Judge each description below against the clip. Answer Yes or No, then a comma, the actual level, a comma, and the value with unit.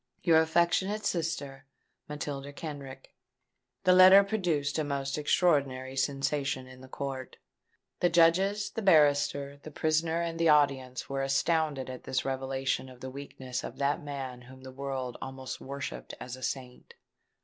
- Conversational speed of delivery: Yes, average, 150 wpm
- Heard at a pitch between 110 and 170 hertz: Yes, medium, 140 Hz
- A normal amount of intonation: Yes, average, 3.5 semitones